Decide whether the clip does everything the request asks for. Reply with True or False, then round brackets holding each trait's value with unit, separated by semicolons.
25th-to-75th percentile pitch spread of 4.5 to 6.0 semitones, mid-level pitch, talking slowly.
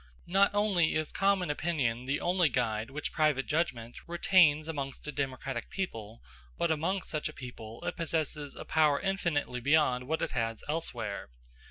False (5.2 semitones; 150 Hz; 160 wpm)